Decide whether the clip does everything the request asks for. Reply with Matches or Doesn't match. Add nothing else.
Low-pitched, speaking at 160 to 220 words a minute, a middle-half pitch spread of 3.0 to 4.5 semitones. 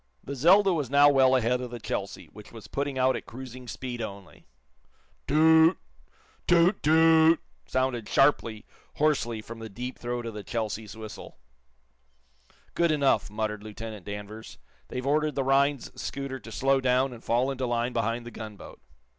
Matches